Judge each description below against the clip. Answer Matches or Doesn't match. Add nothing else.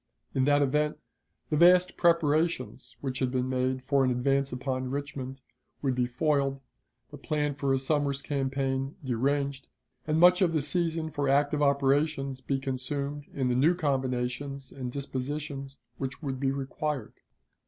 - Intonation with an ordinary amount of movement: Doesn't match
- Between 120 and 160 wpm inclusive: Matches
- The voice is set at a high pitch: Doesn't match